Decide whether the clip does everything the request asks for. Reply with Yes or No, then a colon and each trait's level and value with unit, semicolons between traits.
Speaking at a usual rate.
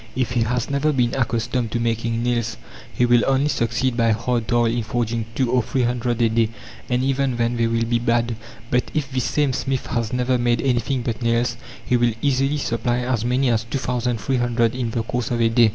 No: fast, 225 wpm